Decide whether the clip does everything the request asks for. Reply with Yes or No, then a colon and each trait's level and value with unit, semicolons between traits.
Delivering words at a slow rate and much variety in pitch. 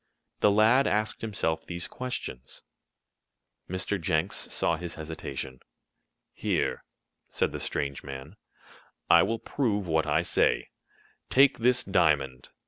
Yes: slow, 120 wpm; wide, 6.0 semitones